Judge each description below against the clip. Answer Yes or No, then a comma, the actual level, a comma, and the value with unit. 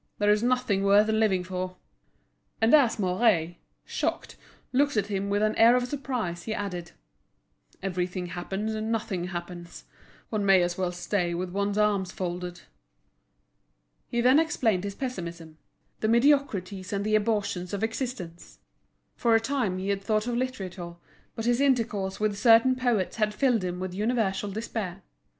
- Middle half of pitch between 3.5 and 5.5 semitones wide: Yes, average, 3.8 semitones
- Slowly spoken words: No, average, 155 wpm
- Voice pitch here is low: No, high, 205 Hz